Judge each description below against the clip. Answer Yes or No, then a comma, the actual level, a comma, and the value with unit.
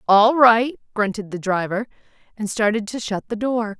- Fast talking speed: No, average, 175 wpm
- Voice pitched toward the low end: No, high, 220 Hz